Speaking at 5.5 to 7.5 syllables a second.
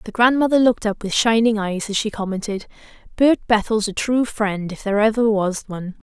Yes: 5.7 syllables/s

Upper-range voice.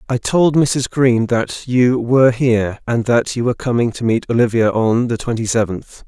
No: low, 120 Hz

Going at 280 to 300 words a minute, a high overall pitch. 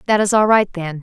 Yes: fast, 295 wpm; high, 195 Hz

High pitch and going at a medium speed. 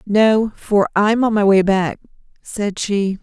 Yes: high, 205 Hz; average, 165 wpm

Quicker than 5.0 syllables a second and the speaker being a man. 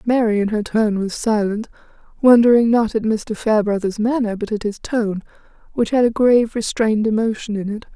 No: 5.5 syllables/s; female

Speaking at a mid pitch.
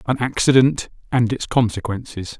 No: low, 115 Hz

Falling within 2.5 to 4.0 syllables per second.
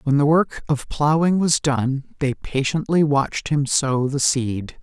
Yes: 3.9 syllables/s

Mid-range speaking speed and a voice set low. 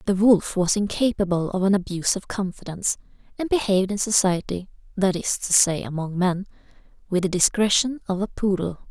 No: average, 170 wpm; high, 195 Hz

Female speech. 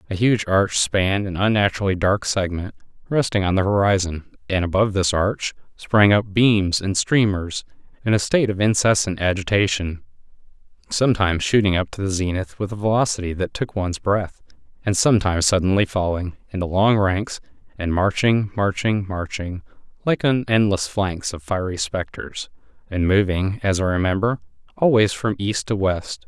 No: male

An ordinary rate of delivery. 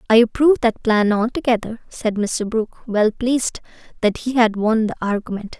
Yes: average, 170 wpm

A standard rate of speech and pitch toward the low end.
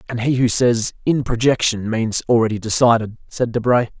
Yes: average, 165 wpm; low, 115 Hz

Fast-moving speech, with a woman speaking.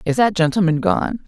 No: average, 190 wpm; female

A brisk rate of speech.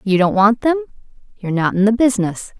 No: average, 185 wpm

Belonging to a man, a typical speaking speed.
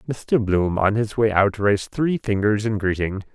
Yes: male; average, 195 wpm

